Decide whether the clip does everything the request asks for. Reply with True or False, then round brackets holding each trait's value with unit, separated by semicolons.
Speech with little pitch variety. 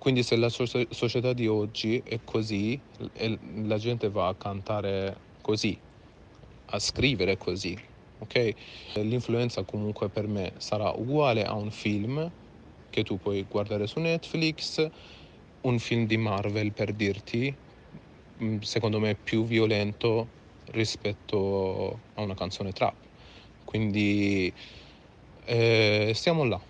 True (2.2 semitones)